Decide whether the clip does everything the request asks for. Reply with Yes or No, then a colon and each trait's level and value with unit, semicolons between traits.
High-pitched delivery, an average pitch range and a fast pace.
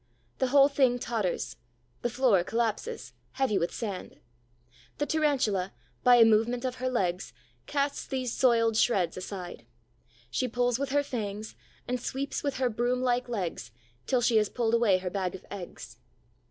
No: high, 235 Hz; average, 4.2 semitones; average, 160 wpm